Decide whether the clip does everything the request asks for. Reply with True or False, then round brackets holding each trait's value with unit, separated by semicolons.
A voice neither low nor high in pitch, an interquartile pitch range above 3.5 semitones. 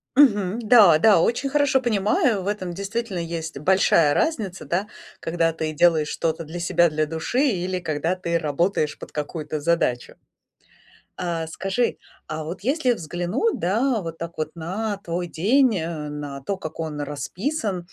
True (175 Hz; 4.8 semitones)